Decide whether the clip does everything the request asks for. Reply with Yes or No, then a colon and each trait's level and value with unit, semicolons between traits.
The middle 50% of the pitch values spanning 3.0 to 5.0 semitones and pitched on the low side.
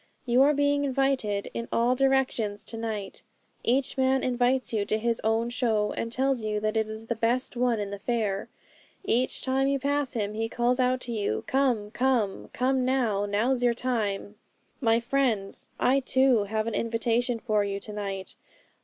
No: average, 3.3 semitones; high, 235 Hz